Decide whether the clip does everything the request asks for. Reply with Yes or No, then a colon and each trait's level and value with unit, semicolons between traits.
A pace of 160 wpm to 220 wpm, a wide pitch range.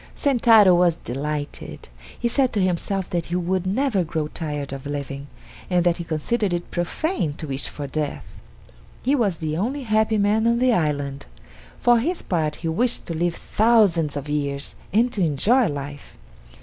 Yes: average, 175 wpm; wide, 6.8 semitones